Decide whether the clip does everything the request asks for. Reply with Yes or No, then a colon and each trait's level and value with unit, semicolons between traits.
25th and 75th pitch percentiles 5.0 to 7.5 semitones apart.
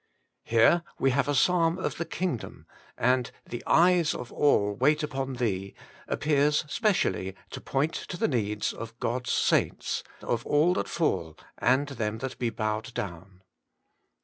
Yes: average, 5.3 semitones